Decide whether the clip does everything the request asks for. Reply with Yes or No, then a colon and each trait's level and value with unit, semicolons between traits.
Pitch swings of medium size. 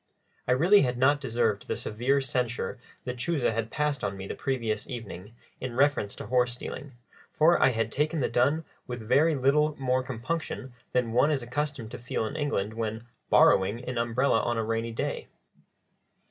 Yes: average, 3.8 semitones